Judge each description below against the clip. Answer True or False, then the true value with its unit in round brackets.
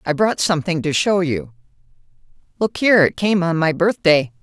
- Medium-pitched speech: True (170 Hz)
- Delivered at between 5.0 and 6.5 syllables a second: True (5.4 syllables/s)